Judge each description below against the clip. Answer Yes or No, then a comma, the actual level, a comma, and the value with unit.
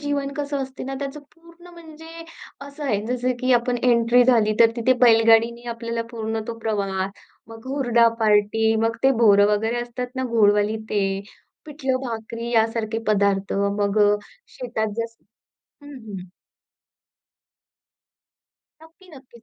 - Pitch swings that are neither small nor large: Yes, average, 3.1 semitones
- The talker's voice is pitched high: Yes, high, 235 Hz